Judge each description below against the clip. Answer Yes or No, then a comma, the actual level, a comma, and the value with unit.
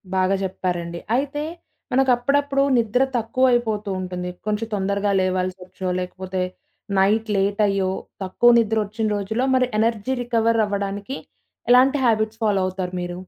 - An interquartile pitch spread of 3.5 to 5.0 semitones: Yes, average, 4.2 semitones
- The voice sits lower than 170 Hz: No, high, 210 Hz